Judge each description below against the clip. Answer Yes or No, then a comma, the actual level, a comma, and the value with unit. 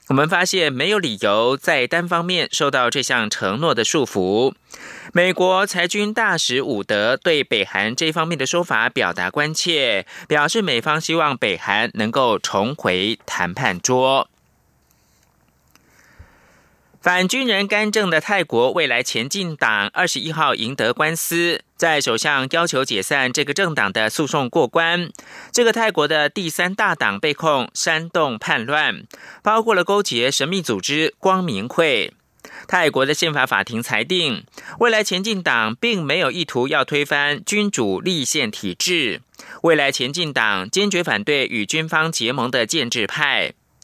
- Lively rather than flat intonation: Yes, wide, 6.5 semitones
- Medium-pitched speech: Yes, medium, 160 Hz